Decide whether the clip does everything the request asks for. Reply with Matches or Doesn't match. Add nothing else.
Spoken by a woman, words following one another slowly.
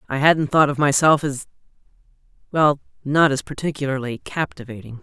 Matches